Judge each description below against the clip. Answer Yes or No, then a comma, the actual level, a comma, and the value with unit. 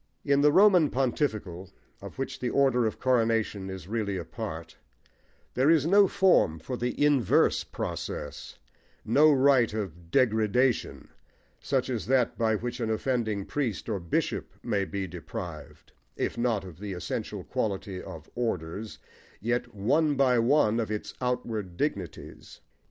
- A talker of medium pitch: No, low, 115 Hz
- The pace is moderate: Yes, average, 145 wpm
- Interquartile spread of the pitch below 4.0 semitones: No, average, 5.1 semitones